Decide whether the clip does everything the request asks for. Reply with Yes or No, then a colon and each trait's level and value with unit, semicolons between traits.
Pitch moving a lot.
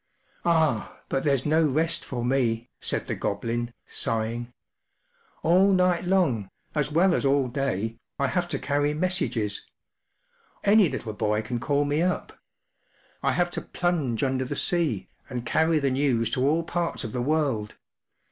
Yes: wide, 5.8 semitones